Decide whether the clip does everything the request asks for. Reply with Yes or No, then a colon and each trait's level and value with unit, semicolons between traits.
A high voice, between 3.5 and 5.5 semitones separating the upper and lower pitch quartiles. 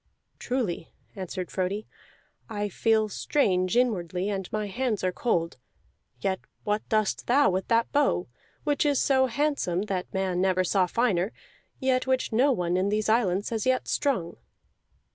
Yes: high, 210 Hz; average, 5.2 semitones